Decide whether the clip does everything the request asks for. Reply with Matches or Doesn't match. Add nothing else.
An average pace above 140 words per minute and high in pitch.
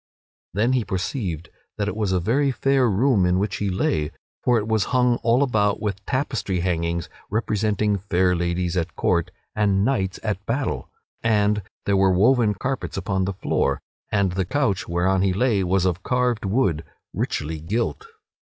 Doesn't match